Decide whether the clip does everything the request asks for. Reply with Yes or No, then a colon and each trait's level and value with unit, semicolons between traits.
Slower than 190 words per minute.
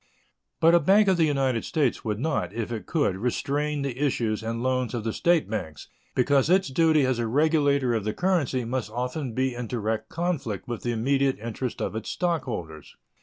No: average, 195 wpm